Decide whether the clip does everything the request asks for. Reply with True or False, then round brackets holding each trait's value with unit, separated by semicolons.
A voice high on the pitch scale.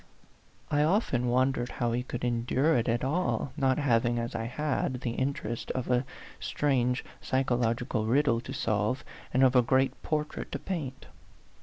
False (125 Hz)